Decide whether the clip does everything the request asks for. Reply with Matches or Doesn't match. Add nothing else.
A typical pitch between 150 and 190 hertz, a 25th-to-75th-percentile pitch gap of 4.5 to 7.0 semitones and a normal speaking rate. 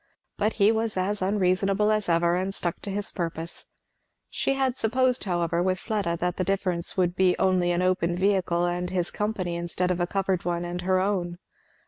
Doesn't match